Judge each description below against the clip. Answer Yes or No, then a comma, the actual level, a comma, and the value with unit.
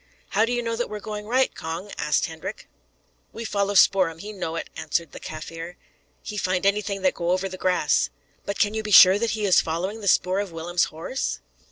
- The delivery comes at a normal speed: No, fast, 220 wpm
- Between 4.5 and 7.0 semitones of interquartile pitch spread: No, average, 3.6 semitones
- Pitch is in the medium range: No, high, 195 Hz